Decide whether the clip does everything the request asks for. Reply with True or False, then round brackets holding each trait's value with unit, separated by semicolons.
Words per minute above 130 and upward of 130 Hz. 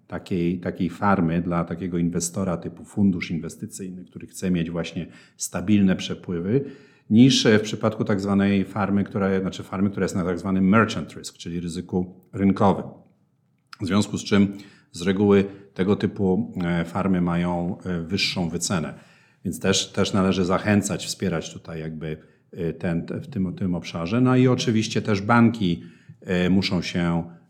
False (155 wpm; 95 Hz)